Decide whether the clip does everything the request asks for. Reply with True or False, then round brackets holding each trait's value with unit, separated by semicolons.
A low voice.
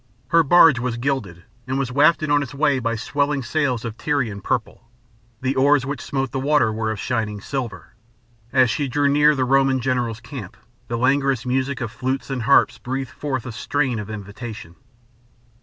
True (130 Hz)